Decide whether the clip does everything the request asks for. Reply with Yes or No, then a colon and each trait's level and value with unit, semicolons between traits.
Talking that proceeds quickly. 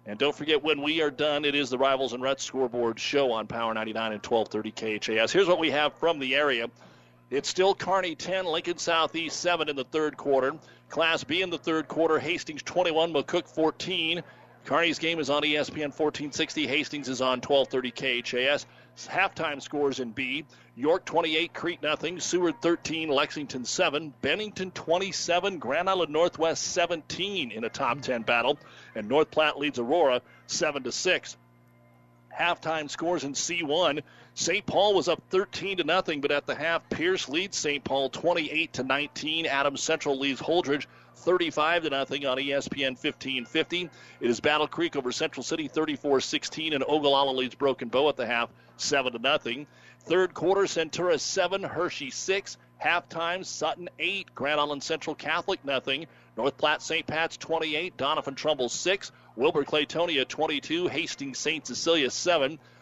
No: average, 165 wpm